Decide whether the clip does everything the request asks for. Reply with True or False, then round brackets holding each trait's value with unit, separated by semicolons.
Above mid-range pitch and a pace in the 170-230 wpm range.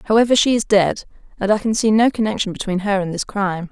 False (205 Hz; 240 wpm)